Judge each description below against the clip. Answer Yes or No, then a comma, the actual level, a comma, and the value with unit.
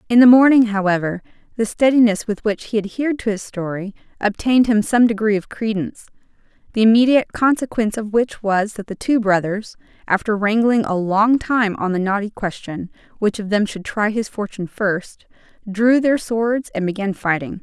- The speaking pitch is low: No, high, 215 Hz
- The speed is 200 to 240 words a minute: No, average, 175 wpm